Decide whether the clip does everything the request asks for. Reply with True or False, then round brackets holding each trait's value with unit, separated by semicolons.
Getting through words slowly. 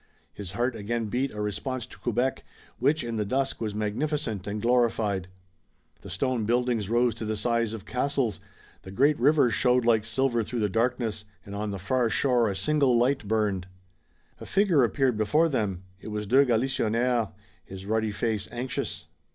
False (175 wpm)